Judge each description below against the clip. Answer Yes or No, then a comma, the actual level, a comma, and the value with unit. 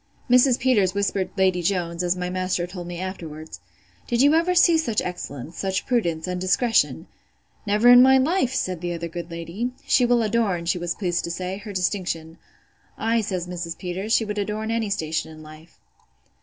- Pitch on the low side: No, medium, 185 Hz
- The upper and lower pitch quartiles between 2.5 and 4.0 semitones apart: No, average, 4.7 semitones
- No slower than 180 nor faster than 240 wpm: Yes, average, 185 wpm